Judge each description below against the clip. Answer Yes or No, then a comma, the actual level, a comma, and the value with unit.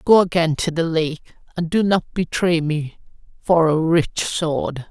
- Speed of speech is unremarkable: Yes, average, 170 wpm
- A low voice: No, medium, 165 Hz